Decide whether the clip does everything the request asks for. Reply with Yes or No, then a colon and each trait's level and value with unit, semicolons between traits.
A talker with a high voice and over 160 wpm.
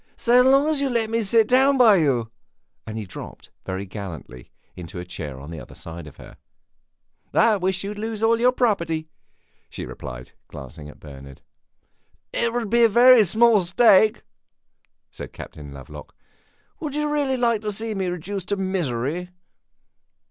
Yes: high, 195 Hz; average, 170 wpm